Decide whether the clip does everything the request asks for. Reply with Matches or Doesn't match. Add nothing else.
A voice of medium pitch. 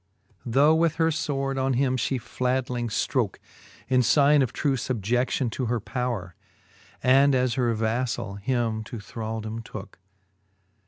Doesn't match